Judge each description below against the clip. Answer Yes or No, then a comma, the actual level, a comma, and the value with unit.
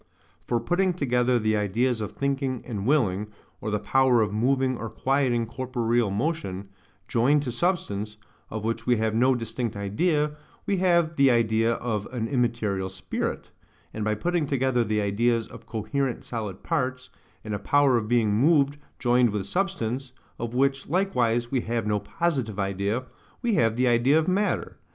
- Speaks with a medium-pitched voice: No, low, 120 Hz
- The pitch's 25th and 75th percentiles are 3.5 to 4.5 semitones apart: Yes, average, 4.0 semitones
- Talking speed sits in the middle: Yes, average, 165 wpm